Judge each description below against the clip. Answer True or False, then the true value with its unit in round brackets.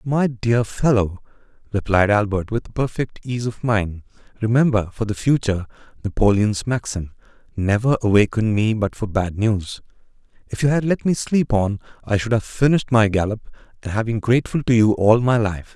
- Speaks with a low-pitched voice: True (110 Hz)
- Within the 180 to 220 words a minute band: False (170 wpm)